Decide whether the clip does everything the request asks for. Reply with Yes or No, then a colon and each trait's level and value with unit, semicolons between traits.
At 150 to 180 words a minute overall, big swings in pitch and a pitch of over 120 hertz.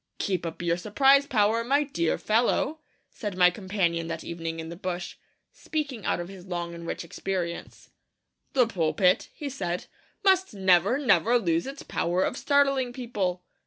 Yes: average, 160 wpm; wide, 6.4 semitones; high, 190 Hz